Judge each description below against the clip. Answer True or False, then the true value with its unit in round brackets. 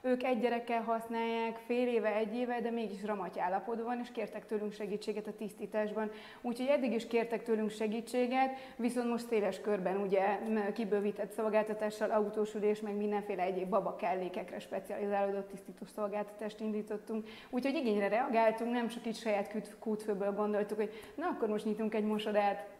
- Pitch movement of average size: False (1.7 semitones)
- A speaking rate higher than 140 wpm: True (150 wpm)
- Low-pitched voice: False (215 Hz)